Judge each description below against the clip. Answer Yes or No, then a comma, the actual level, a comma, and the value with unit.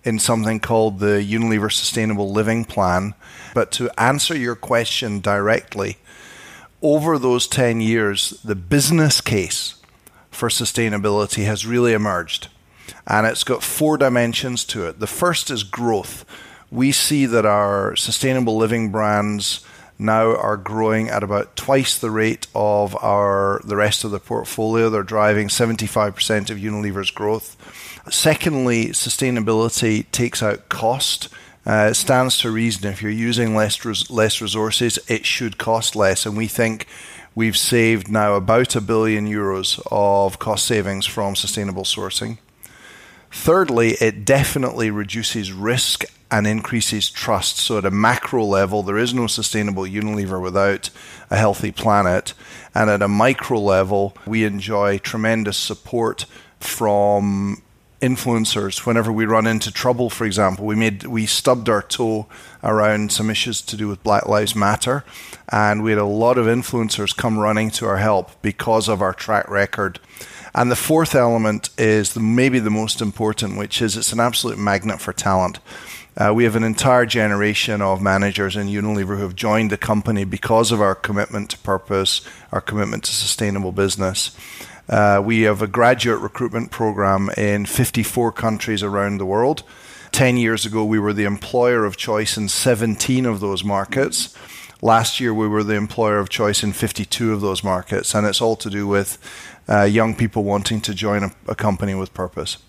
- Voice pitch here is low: Yes, low, 110 Hz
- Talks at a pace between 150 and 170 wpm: Yes, average, 160 wpm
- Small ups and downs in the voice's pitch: Yes, narrow, 2.1 semitones